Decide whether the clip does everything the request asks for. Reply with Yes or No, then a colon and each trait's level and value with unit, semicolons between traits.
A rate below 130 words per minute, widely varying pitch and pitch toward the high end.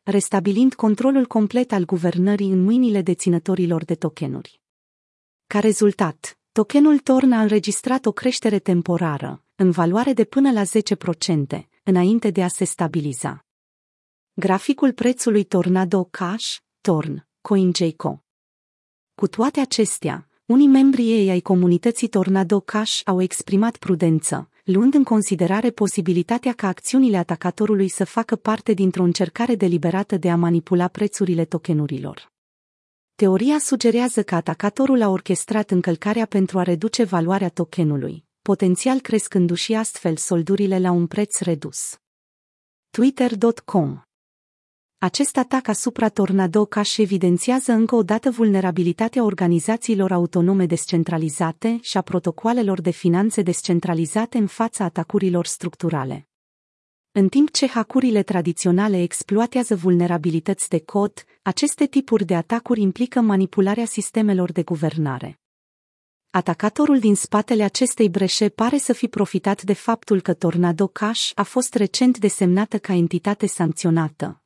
No: average, 120 wpm; average, 4.1 semitones; high, 200 Hz